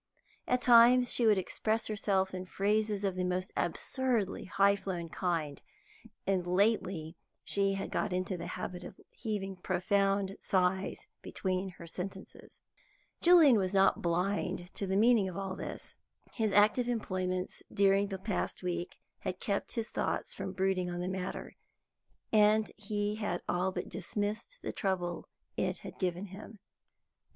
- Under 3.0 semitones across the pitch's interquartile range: Yes, narrow, 2.4 semitones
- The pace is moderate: Yes, average, 150 wpm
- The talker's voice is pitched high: Yes, high, 195 Hz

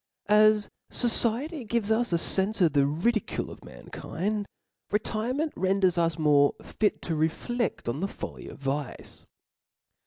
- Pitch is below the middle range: No, high, 195 Hz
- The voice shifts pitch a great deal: Yes, wide, 6.0 semitones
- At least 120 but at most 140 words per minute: Yes, slow, 135 wpm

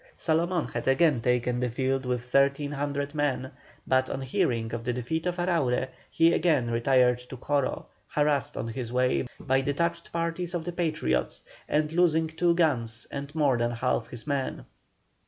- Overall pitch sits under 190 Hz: Yes, medium, 140 Hz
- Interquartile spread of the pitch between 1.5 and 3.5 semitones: No, average, 4.5 semitones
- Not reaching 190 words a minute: Yes, average, 165 wpm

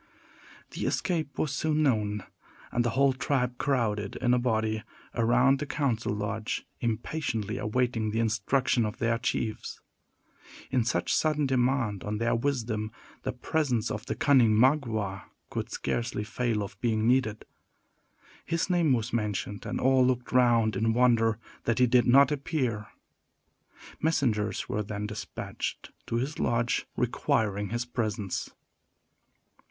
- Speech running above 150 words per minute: No, average, 140 wpm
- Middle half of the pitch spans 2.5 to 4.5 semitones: Yes, average, 3.3 semitones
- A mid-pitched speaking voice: No, low, 120 Hz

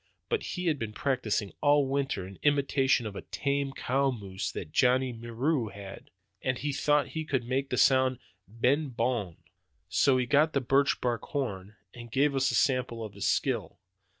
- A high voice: No, low, 130 Hz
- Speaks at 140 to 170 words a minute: No, average, 180 wpm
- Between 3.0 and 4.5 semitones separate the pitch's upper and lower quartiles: Yes, average, 3.5 semitones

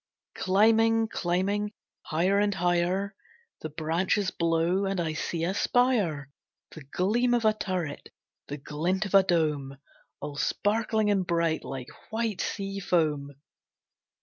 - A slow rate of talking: Yes, slow, 130 wpm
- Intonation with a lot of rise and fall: No, average, 4.4 semitones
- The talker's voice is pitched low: No, medium, 185 Hz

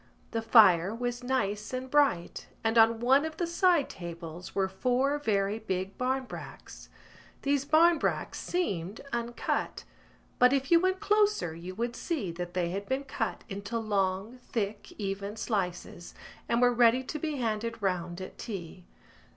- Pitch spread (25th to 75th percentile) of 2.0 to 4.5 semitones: No, wide, 5.4 semitones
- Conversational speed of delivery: Yes, average, 150 wpm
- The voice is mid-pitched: No, high, 225 Hz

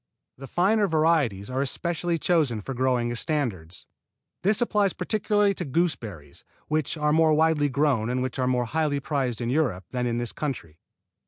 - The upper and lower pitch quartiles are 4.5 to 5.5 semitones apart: Yes, average, 5.1 semitones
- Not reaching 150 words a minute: No, average, 170 wpm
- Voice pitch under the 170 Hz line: Yes, medium, 140 Hz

